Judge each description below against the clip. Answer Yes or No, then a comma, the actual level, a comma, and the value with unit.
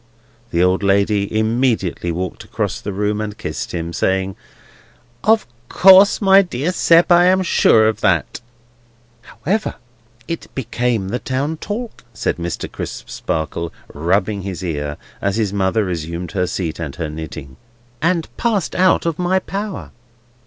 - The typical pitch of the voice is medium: No, low, 105 Hz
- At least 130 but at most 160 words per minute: Yes, average, 145 wpm